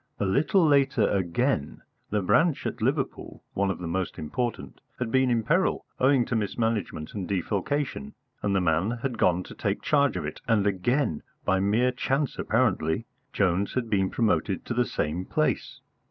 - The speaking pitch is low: Yes, low, 110 Hz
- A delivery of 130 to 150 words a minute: No, average, 170 wpm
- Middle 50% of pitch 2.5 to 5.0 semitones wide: No, wide, 5.4 semitones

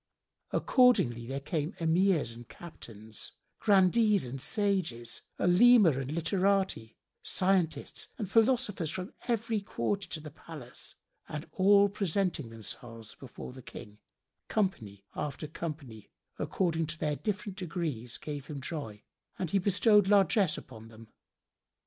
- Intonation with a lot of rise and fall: Yes, wide, 7.6 semitones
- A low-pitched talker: No, medium, 165 Hz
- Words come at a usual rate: No, slow, 125 wpm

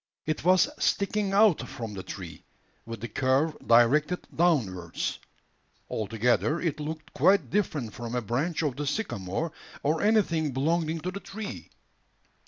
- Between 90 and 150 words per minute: Yes, average, 140 wpm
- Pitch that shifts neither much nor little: No, wide, 6.8 semitones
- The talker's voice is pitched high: No, medium, 150 Hz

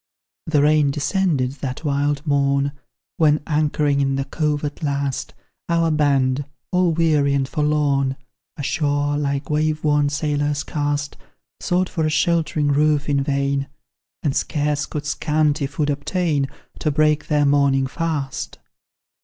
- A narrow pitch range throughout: Yes, narrow, 1.5 semitones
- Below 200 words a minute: Yes, slow, 135 wpm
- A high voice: No, medium, 145 Hz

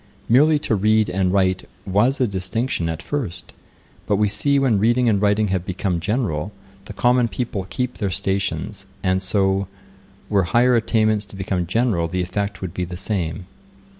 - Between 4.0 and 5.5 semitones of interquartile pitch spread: No, average, 3.5 semitones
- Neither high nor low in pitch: No, low, 100 Hz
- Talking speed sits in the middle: Yes, average, 170 wpm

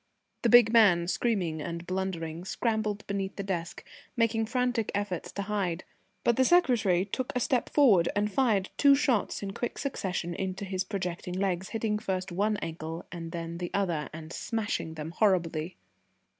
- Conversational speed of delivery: Yes, average, 165 wpm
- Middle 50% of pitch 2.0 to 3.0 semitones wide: No, average, 4.3 semitones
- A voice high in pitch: Yes, high, 195 Hz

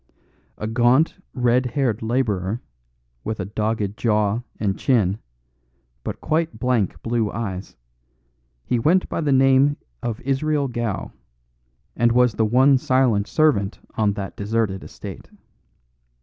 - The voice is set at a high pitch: No, low, 120 Hz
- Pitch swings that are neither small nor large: Yes, average, 3.8 semitones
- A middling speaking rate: No, slow, 125 wpm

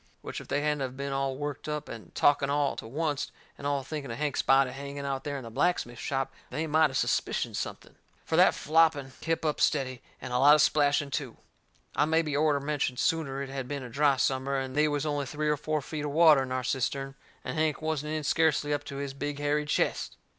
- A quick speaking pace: Yes, fast, 235 wpm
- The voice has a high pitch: No, medium, 145 Hz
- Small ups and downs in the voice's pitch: Yes, narrow, 1.9 semitones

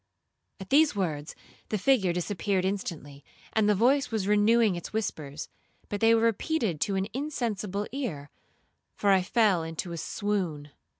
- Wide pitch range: No, average, 4.5 semitones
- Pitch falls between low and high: No, high, 200 Hz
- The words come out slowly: No, average, 155 wpm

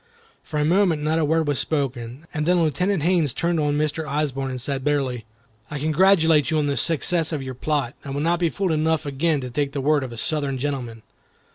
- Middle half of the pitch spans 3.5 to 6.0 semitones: No, average, 2.8 semitones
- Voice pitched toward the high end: No, medium, 150 Hz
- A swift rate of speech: Yes, fast, 225 wpm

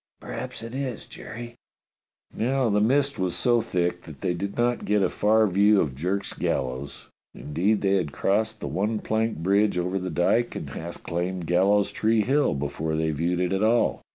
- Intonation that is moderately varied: Yes, average, 4.2 semitones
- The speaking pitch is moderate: No, low, 100 Hz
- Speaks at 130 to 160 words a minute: No, average, 185 wpm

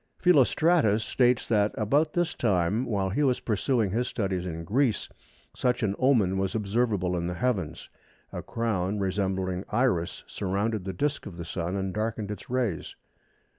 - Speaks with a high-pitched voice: No, low, 105 Hz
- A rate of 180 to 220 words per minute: No, average, 160 wpm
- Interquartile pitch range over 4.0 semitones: Yes, average, 4.6 semitones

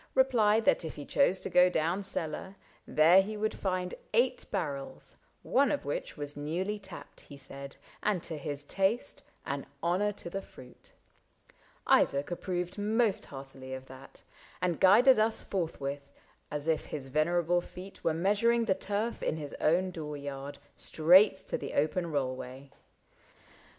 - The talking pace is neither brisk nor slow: Yes, average, 155 wpm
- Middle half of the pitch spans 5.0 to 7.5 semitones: Yes, wide, 5.6 semitones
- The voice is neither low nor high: Yes, medium, 175 Hz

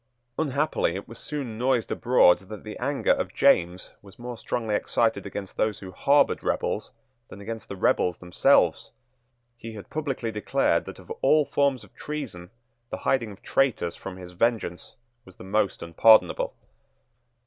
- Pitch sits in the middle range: No, low, 110 Hz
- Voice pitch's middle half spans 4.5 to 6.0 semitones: Yes, average, 5.1 semitones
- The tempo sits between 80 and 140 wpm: No, average, 160 wpm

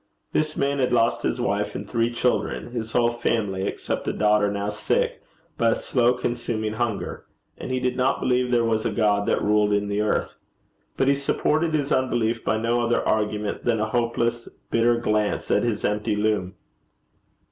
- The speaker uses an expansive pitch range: No, narrow, 2.4 semitones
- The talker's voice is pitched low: Yes, low, 115 Hz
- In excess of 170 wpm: Yes, average, 185 wpm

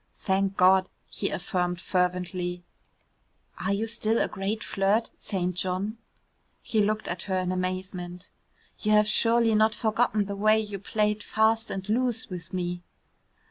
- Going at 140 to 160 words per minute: Yes, average, 145 wpm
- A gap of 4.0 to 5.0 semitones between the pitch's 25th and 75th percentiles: No, average, 2.9 semitones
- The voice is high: Yes, high, 195 Hz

